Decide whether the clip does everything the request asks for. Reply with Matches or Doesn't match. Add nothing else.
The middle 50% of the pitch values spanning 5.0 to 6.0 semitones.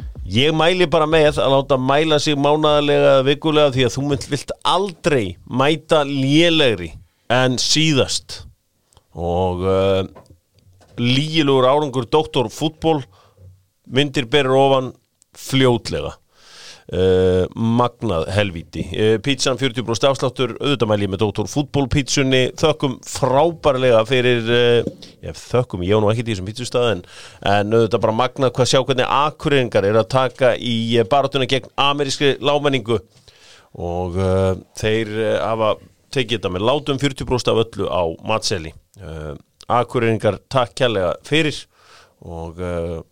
Matches